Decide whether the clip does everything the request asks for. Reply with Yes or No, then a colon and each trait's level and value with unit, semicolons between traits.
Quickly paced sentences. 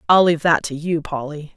Yes: fast, 230 wpm